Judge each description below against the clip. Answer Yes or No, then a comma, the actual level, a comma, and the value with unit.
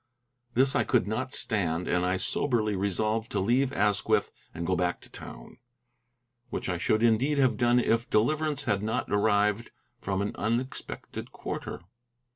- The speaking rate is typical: Yes, average, 155 wpm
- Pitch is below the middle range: Yes, low, 110 Hz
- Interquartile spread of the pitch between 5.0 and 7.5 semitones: No, average, 3.7 semitones